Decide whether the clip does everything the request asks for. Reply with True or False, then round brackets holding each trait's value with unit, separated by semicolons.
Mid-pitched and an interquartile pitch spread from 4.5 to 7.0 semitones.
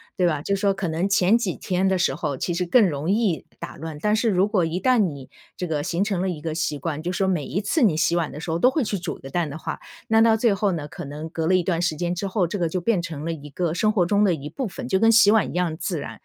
False (180 Hz; 3.9 semitones)